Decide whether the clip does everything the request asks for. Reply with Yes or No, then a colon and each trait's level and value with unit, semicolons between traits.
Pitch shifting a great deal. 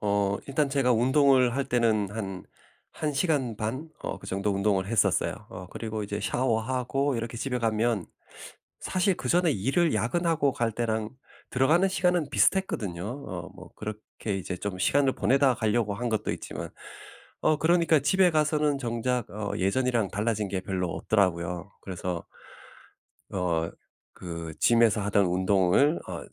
Yes: wide, 5.7 semitones